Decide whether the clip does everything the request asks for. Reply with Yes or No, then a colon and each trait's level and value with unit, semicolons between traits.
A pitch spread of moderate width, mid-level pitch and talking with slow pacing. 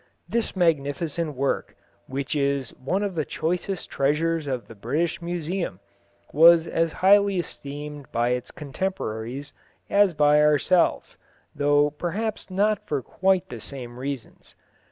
Yes: average, 4.3 semitones; medium, 150 Hz; slow, 130 wpm